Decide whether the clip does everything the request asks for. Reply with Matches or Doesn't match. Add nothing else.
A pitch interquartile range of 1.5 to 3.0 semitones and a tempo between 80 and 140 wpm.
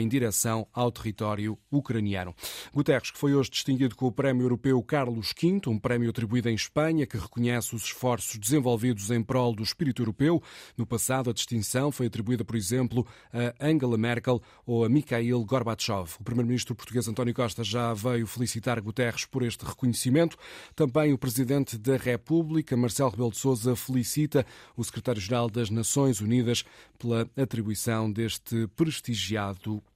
Doesn't match